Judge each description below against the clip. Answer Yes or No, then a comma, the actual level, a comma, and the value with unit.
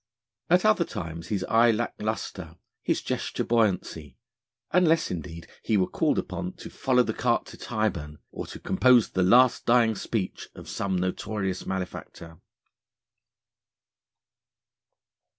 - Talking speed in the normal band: No, slow, 130 wpm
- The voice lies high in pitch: No, low, 110 Hz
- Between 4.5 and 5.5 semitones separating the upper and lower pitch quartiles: Yes, average, 5.0 semitones